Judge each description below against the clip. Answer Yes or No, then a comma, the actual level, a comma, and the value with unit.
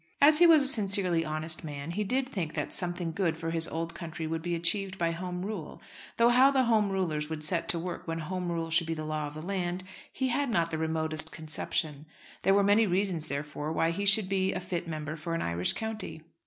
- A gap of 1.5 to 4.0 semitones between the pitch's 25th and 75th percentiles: Yes, average, 3.7 semitones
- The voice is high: No, medium, 170 Hz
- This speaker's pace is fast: Yes, fast, 235 wpm